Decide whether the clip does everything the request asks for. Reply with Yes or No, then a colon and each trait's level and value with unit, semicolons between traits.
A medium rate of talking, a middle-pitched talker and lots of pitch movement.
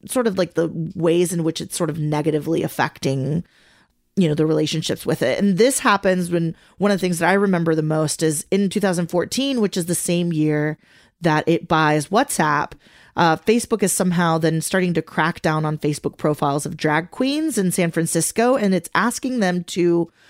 No: average, 195 wpm; medium, 170 Hz; average, 3.7 semitones